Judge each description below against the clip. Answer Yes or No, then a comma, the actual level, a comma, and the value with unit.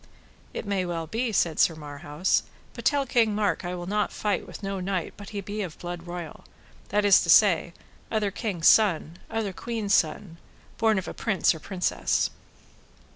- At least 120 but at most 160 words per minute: No, average, 185 wpm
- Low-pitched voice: No, high, 195 Hz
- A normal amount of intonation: Yes, average, 3.4 semitones